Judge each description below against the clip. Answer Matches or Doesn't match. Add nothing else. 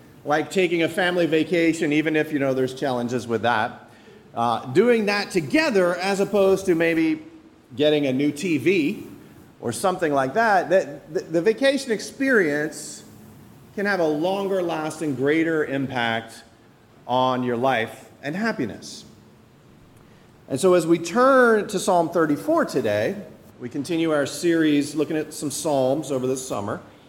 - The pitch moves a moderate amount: Doesn't match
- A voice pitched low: Doesn't match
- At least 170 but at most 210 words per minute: Doesn't match